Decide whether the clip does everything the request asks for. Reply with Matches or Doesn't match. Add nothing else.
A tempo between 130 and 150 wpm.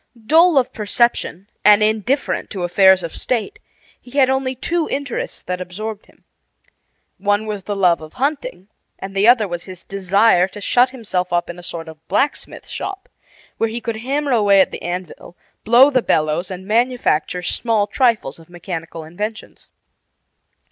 Doesn't match